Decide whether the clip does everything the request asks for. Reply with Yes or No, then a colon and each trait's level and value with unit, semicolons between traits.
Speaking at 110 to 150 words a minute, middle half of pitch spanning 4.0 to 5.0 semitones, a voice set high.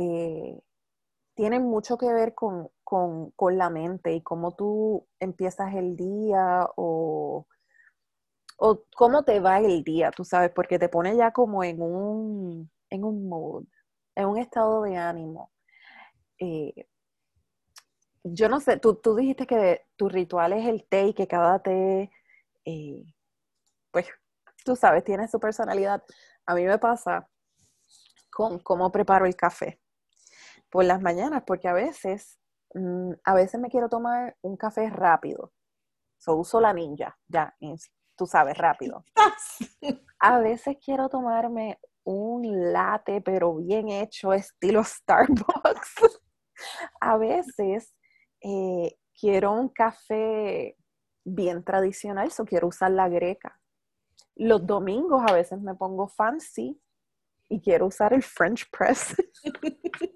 Yes: average, 135 wpm; average, 4.4 semitones; high, 200 Hz